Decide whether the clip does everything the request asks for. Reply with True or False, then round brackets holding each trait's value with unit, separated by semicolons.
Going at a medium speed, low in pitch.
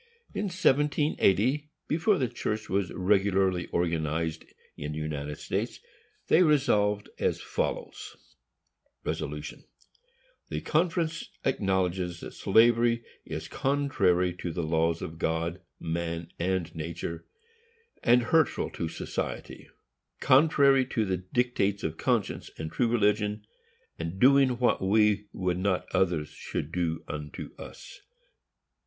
False (115 wpm; 95 Hz)